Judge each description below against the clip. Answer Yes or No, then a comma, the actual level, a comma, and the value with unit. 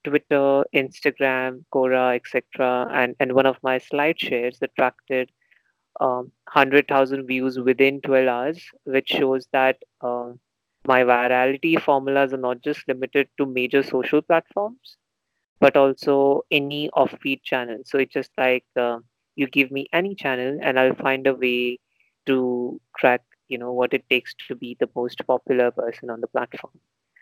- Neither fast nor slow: Yes, average, 150 wpm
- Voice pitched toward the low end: Yes, low, 130 Hz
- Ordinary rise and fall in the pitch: No, narrow, 1.8 semitones